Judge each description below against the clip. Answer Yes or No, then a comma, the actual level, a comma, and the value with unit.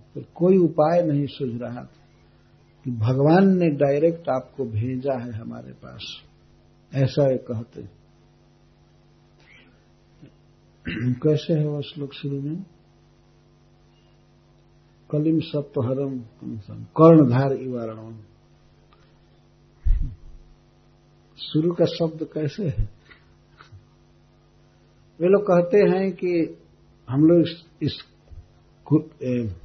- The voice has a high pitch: No, medium, 145 Hz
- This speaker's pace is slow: Yes, slow, 90 wpm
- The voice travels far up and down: No, average, 4.9 semitones